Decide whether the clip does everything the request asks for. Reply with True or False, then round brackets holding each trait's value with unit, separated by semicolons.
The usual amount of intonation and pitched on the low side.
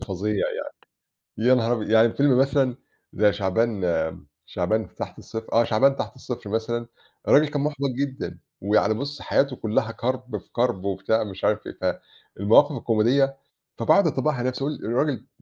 True (4.1 semitones; 115 Hz)